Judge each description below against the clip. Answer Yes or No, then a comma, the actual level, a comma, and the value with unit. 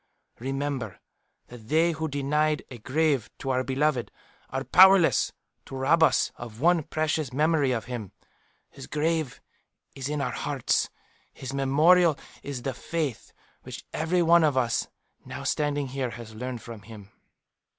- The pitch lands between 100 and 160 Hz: Yes, medium, 140 Hz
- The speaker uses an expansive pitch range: No, average, 3.9 semitones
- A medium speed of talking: Yes, average, 150 wpm